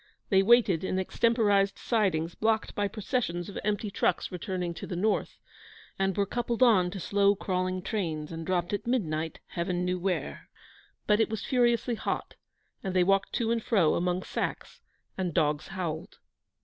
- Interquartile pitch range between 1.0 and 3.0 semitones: No, average, 3.5 semitones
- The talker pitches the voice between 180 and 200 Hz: Yes, high, 190 Hz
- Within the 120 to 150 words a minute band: No, average, 165 wpm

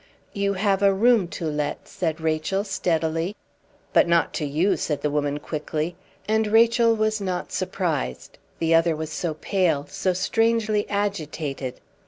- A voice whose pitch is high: No, medium, 175 Hz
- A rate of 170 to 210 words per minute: No, average, 150 wpm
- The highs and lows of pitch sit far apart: No, average, 4.6 semitones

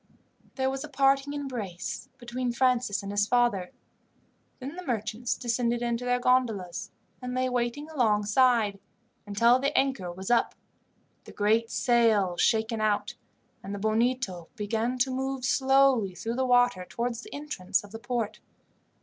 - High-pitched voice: Yes, high, 240 Hz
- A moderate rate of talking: Yes, average, 150 wpm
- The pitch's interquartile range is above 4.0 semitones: No, average, 3.5 semitones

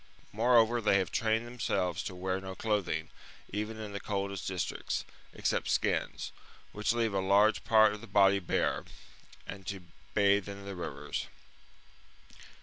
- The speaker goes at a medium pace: Yes, average, 145 wpm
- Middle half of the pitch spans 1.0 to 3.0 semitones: Yes, narrow, 2.4 semitones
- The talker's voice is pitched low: Yes, low, 100 Hz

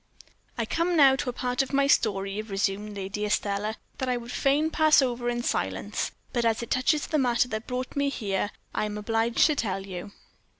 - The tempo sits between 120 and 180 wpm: No, fast, 205 wpm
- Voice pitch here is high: Yes, high, 235 Hz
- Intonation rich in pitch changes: No, average, 4.3 semitones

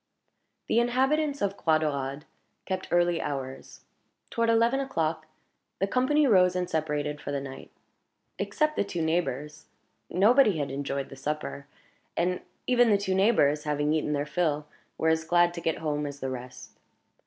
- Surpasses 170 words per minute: No, average, 160 wpm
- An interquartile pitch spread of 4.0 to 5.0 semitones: No, wide, 5.4 semitones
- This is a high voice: No, medium, 160 Hz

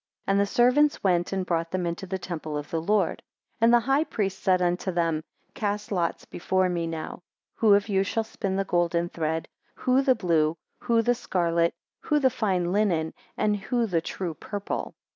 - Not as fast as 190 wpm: No, average, 195 wpm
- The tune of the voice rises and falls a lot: No, average, 4.1 semitones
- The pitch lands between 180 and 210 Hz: Yes, high, 190 Hz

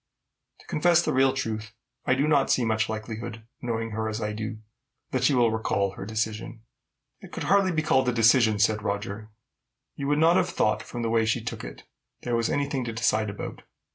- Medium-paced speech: No, fast, 210 wpm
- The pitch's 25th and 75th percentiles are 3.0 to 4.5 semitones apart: Yes, average, 3.3 semitones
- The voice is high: No, low, 115 Hz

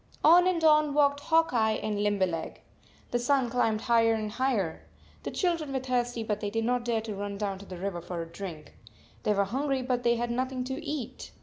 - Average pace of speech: No, fast, 230 wpm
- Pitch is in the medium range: No, high, 235 Hz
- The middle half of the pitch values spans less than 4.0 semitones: No, average, 4.6 semitones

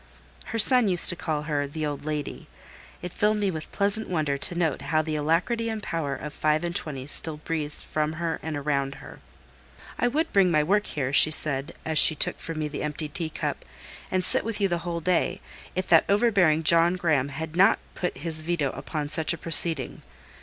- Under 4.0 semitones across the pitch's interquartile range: Yes, average, 3.0 semitones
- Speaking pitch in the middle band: Yes, medium, 160 Hz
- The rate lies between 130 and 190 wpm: No, fast, 205 wpm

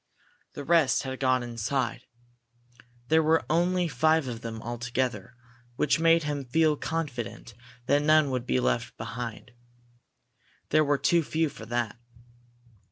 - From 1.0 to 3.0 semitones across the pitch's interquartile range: No, average, 4.6 semitones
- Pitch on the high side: No, low, 135 Hz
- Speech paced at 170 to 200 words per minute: No, slow, 135 wpm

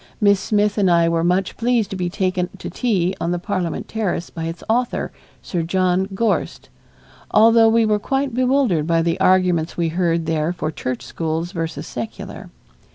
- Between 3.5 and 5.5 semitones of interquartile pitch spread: Yes, average, 4.2 semitones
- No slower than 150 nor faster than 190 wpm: Yes, average, 175 wpm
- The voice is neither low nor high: Yes, medium, 180 Hz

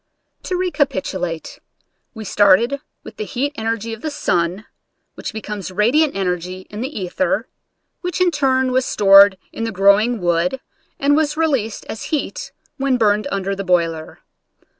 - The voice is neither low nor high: No, high, 220 Hz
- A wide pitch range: Yes, wide, 6.6 semitones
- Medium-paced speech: Yes, average, 150 wpm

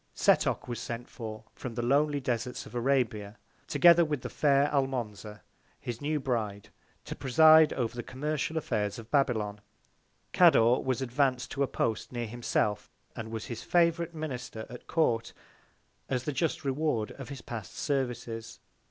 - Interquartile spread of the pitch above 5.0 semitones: No, average, 3.9 semitones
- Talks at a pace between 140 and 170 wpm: Yes, average, 155 wpm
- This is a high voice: No, low, 125 Hz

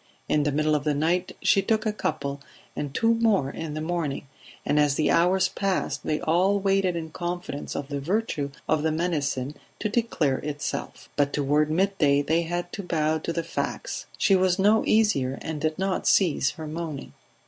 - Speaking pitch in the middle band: Yes, medium, 160 Hz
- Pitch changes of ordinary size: Yes, average, 4.2 semitones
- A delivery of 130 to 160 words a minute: No, average, 190 wpm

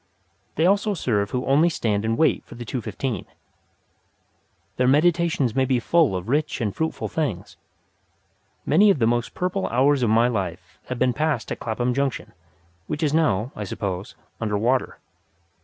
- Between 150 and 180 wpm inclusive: Yes, average, 170 wpm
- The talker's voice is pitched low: Yes, low, 125 Hz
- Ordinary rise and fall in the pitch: No, wide, 5.7 semitones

